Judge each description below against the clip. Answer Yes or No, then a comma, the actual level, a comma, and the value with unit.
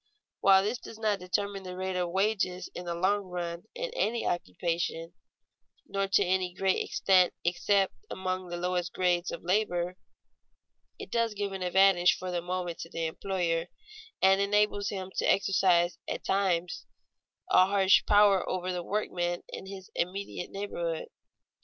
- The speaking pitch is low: No, medium, 185 Hz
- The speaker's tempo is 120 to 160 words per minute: Yes, average, 155 wpm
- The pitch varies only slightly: Yes, narrow, 1.9 semitones